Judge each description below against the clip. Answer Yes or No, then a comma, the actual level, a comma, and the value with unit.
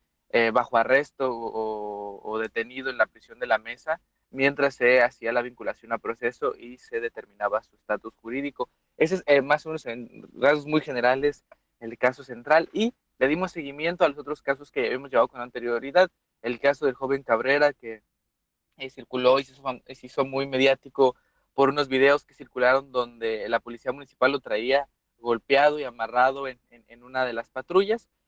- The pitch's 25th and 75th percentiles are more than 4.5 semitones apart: No, average, 2.8 semitones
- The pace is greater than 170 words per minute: Yes, average, 185 wpm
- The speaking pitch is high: No, low, 130 Hz